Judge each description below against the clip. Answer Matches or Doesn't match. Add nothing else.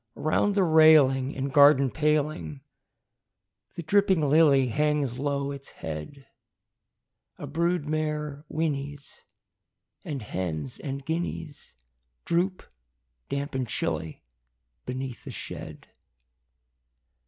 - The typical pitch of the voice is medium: Matches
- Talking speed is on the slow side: Matches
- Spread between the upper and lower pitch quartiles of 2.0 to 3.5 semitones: Matches